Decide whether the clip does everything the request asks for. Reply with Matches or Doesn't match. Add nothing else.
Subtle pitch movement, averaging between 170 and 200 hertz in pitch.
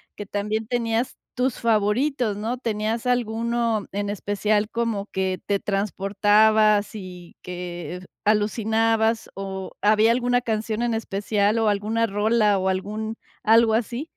Doesn't match